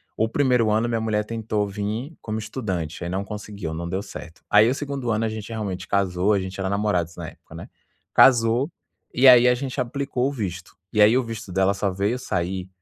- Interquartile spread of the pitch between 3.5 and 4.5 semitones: Yes, average, 3.8 semitones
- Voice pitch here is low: Yes, low, 105 Hz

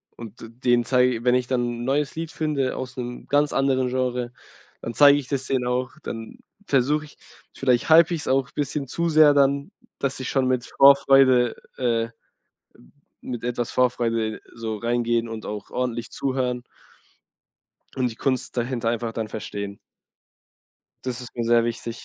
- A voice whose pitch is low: Yes, low, 125 Hz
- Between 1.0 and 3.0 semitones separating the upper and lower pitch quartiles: Yes, narrow, 2.4 semitones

